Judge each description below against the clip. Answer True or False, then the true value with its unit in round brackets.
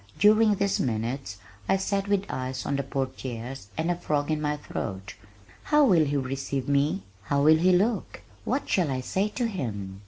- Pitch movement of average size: False (6.8 semitones)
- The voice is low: False (145 Hz)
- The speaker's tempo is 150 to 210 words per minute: True (185 wpm)